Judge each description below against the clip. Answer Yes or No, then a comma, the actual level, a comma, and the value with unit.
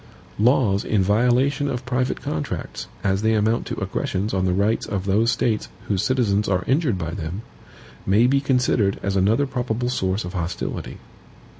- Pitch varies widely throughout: No, average, 4.4 semitones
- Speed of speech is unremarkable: Yes, average, 165 wpm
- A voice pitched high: No, low, 110 Hz